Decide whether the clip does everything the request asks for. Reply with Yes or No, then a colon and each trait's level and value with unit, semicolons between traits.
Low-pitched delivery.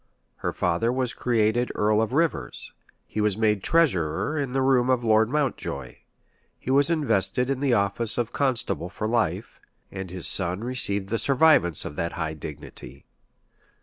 Yes: low, 110 Hz